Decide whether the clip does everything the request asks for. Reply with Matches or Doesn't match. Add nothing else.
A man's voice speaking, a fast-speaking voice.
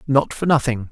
Doesn't match